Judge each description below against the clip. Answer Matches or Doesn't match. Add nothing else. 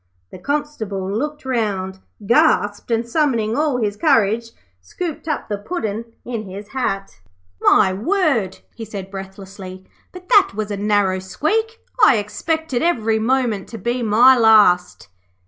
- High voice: Matches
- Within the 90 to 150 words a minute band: Matches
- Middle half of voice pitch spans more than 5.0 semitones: Matches